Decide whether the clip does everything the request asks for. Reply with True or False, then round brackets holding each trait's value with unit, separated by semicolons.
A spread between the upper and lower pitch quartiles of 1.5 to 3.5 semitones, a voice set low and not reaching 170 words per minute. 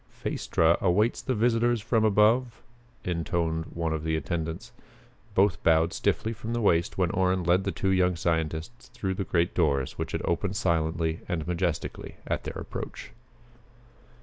False (4.0 semitones; 90 Hz; 155 wpm)